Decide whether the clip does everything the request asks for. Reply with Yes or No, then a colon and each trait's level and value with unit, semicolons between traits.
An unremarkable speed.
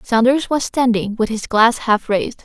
Yes: average, 195 wpm